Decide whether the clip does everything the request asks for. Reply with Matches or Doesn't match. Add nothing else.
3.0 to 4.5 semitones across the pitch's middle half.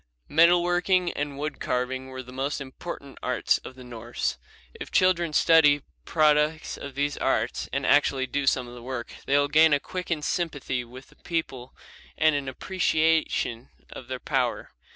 Matches